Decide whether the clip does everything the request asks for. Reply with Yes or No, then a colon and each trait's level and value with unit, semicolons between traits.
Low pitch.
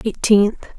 No: high, 210 Hz